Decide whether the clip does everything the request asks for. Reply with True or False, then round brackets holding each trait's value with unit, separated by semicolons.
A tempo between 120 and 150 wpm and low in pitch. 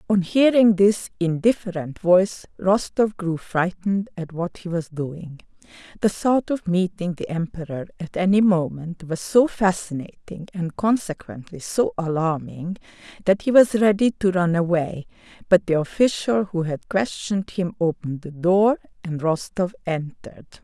False (140 wpm; 180 Hz)